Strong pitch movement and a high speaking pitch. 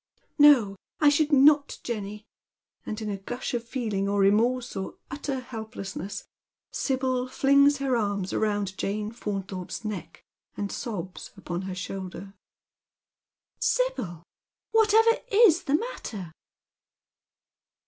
Yes: wide, 6.0 semitones; high, 220 Hz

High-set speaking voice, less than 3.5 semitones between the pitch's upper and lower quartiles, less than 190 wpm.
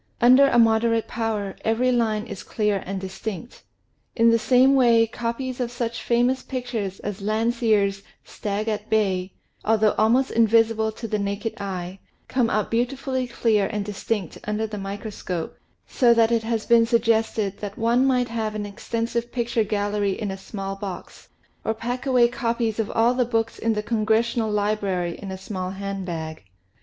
Yes: high, 220 Hz; narrow, 2.6 semitones; average, 175 wpm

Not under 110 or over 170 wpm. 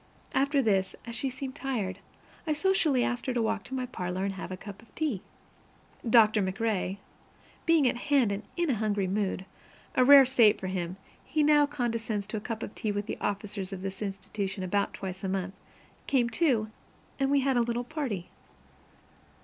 No: average, 190 wpm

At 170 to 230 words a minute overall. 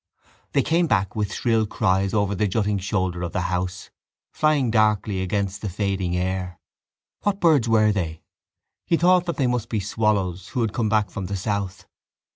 Yes: average, 180 wpm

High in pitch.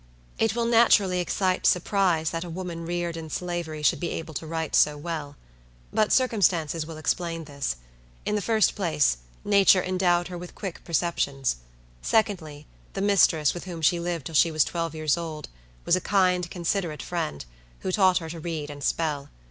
No: medium, 170 Hz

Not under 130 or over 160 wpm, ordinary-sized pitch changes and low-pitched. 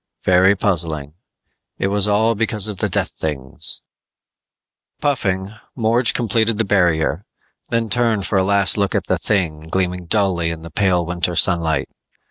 Yes: average, 155 wpm; average, 3.7 semitones; very low, 95 Hz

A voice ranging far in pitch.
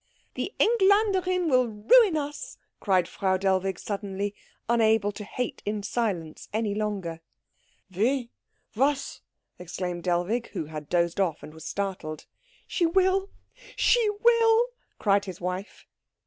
Yes: wide, 8.4 semitones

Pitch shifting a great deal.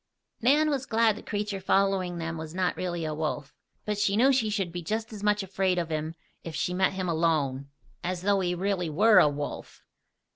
No: average, 4.0 semitones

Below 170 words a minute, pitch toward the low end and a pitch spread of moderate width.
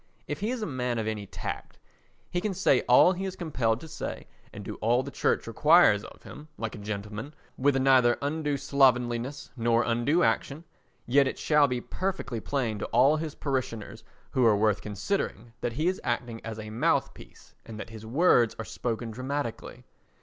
No: average, 180 wpm; low, 125 Hz; average, 4.5 semitones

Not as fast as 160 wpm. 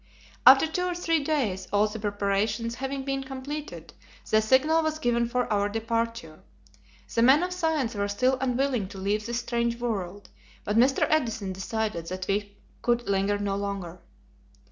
No: average, 165 wpm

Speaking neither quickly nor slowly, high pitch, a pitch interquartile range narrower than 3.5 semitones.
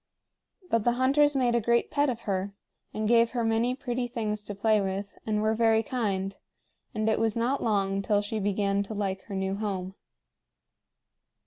Yes: average, 185 wpm; high, 215 Hz; average, 2.9 semitones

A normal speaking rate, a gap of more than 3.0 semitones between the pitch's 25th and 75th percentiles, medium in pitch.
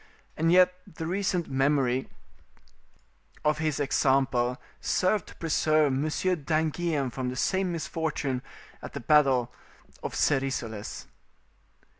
No: slow, 110 wpm; average, 3.7 semitones; medium, 150 Hz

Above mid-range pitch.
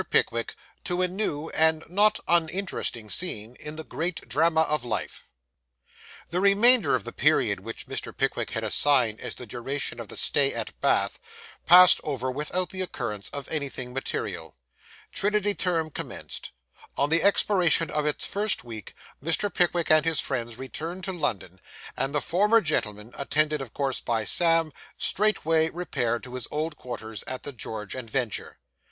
No: medium, 150 Hz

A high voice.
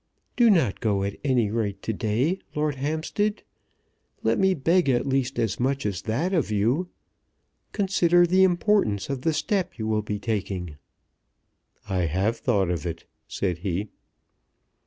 No: low, 120 Hz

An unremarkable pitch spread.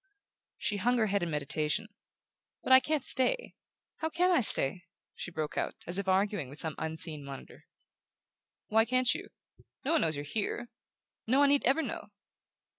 No: wide, 8.5 semitones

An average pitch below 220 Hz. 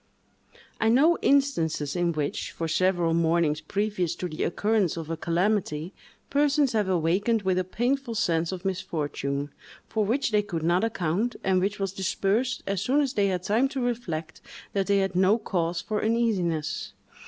Yes: high, 190 Hz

